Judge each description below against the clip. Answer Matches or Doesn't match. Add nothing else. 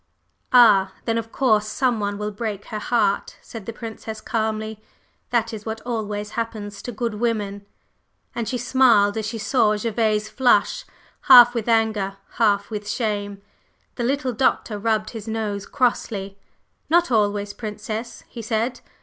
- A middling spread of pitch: Doesn't match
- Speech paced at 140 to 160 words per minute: Matches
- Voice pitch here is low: Doesn't match